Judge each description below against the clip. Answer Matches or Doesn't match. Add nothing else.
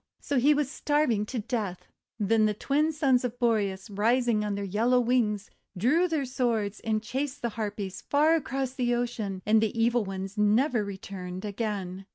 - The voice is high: Matches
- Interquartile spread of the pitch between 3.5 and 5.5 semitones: Matches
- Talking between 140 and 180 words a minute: Matches